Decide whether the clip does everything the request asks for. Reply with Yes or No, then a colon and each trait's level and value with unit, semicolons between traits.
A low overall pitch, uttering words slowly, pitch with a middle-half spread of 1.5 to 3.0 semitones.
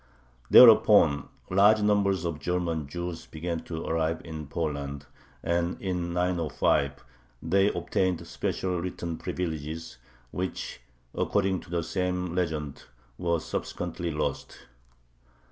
Yes: very low, 85 Hz; slow, 110 wpm; narrow, 2.4 semitones